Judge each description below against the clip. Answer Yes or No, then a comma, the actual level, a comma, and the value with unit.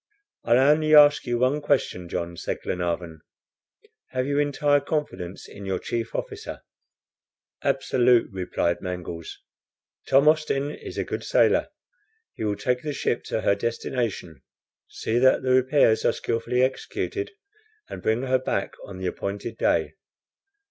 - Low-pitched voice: Yes, low, 120 Hz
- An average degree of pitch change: No, wide, 6.5 semitones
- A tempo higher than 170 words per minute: No, average, 140 wpm